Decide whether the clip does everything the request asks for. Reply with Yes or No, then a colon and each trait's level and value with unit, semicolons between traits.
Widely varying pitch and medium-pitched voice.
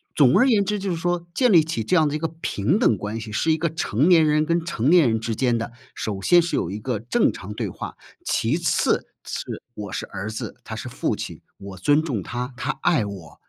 Yes: wide, 7.4 semitones; medium, 145 Hz